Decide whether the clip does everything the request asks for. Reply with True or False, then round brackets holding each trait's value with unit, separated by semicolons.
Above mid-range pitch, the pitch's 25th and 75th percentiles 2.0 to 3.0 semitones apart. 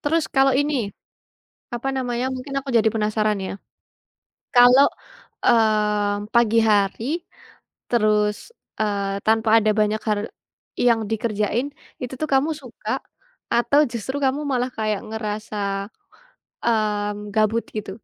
True (220 Hz; 2.7 semitones)